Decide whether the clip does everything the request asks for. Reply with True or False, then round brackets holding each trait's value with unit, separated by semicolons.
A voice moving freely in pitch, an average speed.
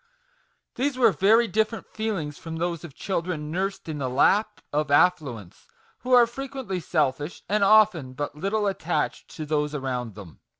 True (6.4 semitones; 160 wpm)